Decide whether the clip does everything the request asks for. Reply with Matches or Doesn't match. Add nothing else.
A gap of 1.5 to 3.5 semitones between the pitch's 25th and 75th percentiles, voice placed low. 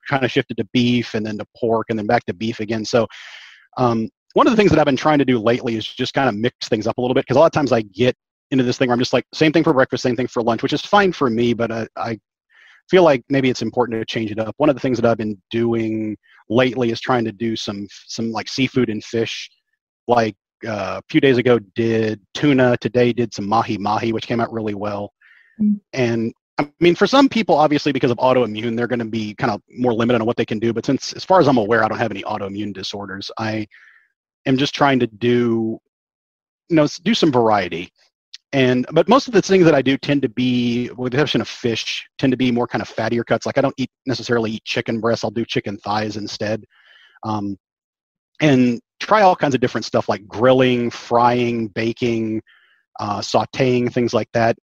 Matches